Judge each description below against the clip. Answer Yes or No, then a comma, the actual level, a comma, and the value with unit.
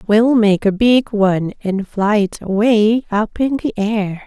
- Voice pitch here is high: Yes, high, 215 Hz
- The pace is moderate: Yes, average, 185 wpm